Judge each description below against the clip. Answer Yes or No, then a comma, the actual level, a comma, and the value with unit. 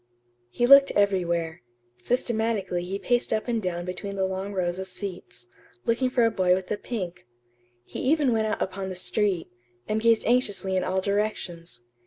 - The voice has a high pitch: Yes, high, 195 Hz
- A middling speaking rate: Yes, average, 175 wpm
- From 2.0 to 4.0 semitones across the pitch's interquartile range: Yes, average, 3.7 semitones